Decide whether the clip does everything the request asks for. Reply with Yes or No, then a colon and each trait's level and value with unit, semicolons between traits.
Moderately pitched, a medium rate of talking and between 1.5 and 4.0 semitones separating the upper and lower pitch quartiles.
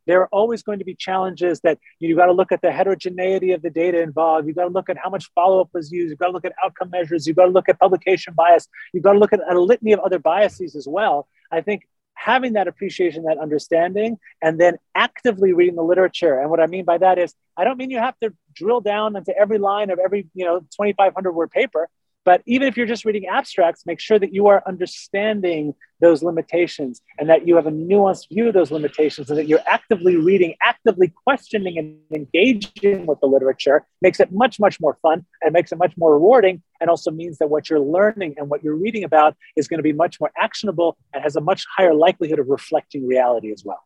No: medium, 180 Hz; fast, 235 wpm; average, 3.4 semitones